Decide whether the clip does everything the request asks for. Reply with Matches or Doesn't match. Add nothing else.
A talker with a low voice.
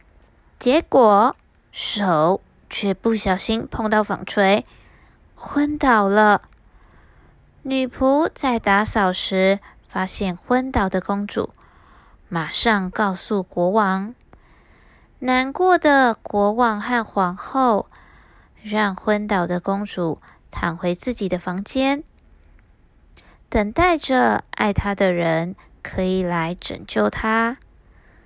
Doesn't match